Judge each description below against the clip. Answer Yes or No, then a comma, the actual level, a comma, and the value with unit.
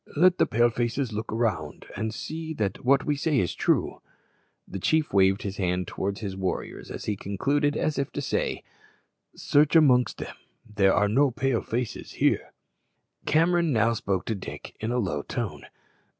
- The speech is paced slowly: No, average, 175 wpm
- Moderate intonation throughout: No, wide, 6.4 semitones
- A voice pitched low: Yes, low, 115 Hz